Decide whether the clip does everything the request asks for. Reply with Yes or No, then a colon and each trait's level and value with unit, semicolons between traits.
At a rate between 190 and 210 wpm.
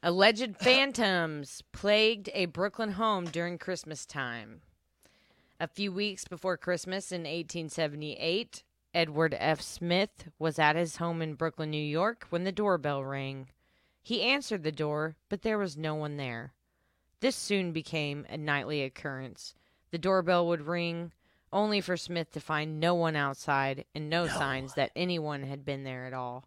No: average, 155 wpm